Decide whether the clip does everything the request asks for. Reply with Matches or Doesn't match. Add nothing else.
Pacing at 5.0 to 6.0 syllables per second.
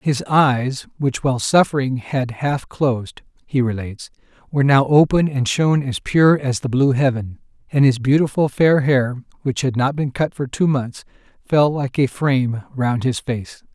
Doesn't match